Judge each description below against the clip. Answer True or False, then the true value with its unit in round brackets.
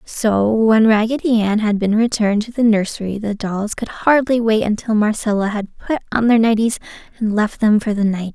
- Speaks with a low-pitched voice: False (215 Hz)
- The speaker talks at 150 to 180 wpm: False (200 wpm)